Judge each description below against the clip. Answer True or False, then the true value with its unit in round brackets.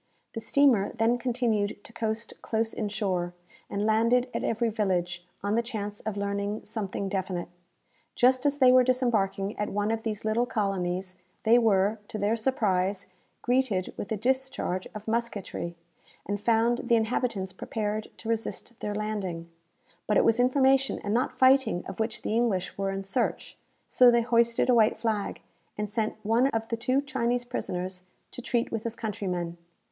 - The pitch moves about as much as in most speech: True (3.1 semitones)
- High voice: True (220 Hz)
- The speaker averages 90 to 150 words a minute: False (170 wpm)